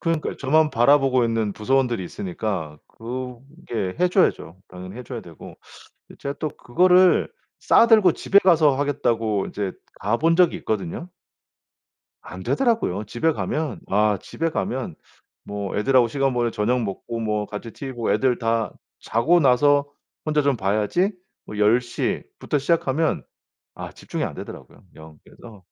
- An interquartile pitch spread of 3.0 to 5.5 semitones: No, wide, 6.1 semitones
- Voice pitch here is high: No, low, 125 Hz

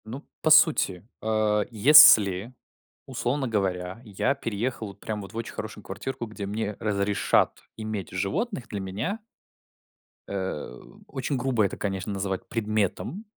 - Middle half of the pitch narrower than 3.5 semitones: No, average, 3.8 semitones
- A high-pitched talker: No, low, 110 Hz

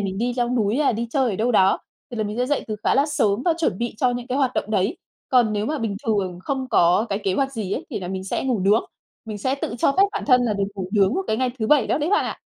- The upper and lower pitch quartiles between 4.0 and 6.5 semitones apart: Yes, average, 4.4 semitones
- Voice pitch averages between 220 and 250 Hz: Yes, high, 230 Hz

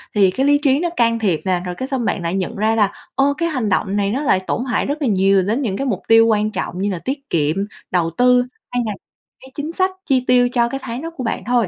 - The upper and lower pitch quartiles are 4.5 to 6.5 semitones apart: Yes, average, 5.2 semitones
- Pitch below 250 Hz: Yes, high, 230 Hz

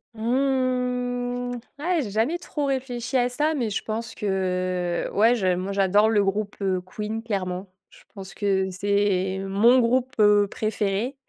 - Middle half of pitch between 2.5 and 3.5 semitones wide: No, average, 4.2 semitones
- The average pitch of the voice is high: Yes, high, 215 Hz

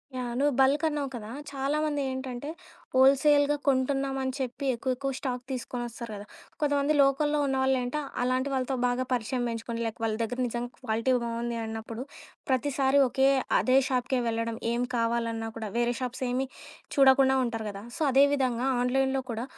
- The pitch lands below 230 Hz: No, very high, 255 Hz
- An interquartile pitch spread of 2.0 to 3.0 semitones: Yes, narrow, 2.4 semitones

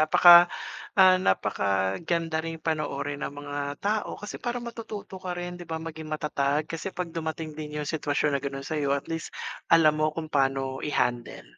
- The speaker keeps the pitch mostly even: No, average, 3.1 semitones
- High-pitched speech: No, medium, 155 Hz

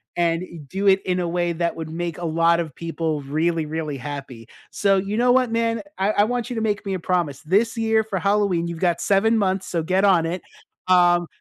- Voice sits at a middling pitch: Yes, medium, 180 Hz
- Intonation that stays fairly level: No, average, 3.6 semitones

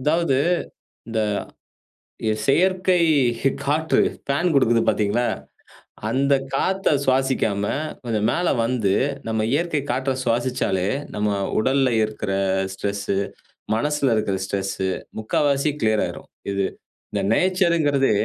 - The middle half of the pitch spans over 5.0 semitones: Yes, wide, 5.4 semitones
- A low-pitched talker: Yes, low, 130 Hz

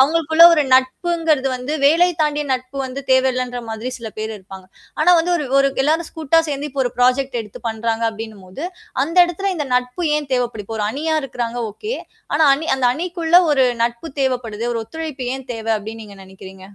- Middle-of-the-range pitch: No, very high, 260 Hz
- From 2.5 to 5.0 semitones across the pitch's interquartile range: No, wide, 5.4 semitones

